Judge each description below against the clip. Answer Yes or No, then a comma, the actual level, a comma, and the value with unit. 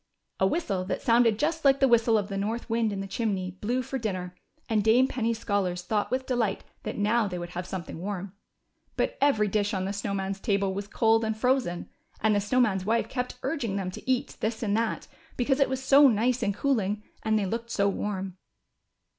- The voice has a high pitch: Yes, high, 215 Hz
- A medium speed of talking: No, fast, 215 wpm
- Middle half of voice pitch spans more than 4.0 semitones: No, average, 3.6 semitones